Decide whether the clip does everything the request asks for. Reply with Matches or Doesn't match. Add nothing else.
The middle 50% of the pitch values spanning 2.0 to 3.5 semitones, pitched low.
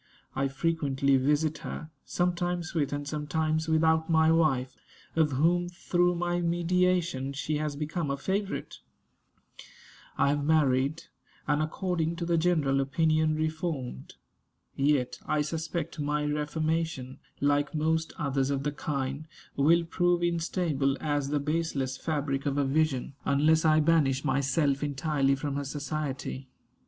Doesn't match